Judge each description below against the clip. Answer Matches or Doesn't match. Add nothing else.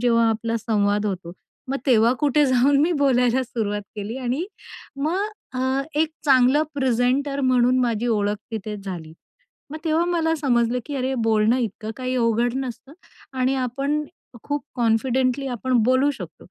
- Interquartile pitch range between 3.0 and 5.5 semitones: Matches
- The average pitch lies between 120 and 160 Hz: Doesn't match